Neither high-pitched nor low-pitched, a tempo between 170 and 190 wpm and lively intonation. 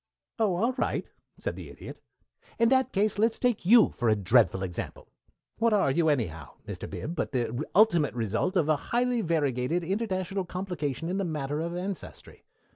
Yes: medium, 175 Hz; average, 175 wpm; wide, 7.2 semitones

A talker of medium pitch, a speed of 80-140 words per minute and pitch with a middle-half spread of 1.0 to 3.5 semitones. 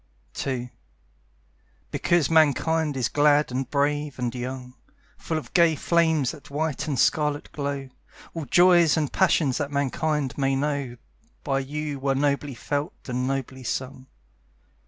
Yes: medium, 145 Hz; slow, 135 wpm; narrow, 2.4 semitones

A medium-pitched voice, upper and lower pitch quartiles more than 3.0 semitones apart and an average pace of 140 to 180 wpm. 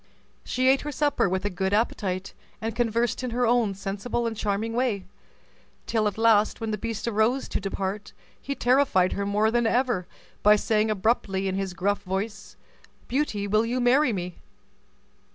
No: high, 215 Hz; average, 3.4 semitones; average, 170 wpm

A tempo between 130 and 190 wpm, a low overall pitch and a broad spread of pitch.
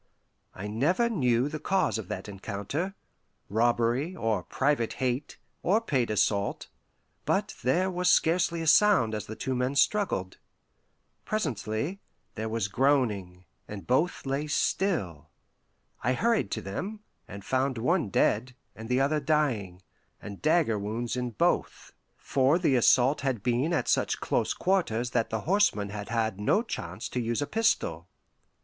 Yes: average, 150 wpm; low, 125 Hz; wide, 6.6 semitones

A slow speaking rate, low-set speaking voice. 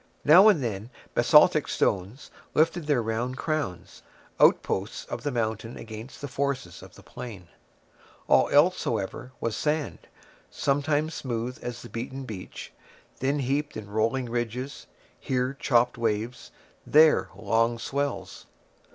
Yes: slow, 130 wpm; low, 125 Hz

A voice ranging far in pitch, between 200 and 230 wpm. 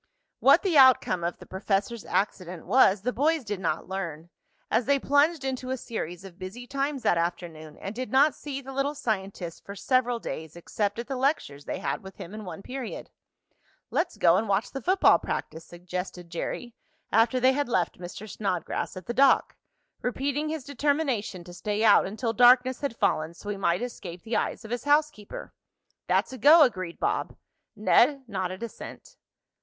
No: wide, 6.3 semitones; average, 180 wpm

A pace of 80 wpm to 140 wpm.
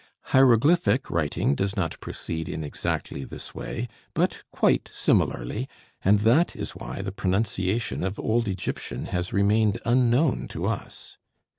Yes: slow, 135 wpm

